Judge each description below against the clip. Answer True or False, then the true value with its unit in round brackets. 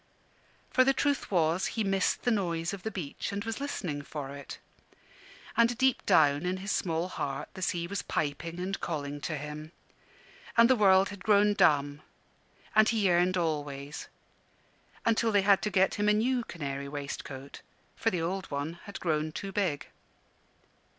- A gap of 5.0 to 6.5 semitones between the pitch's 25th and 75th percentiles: True (5.5 semitones)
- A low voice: False (180 Hz)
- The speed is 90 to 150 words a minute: False (170 wpm)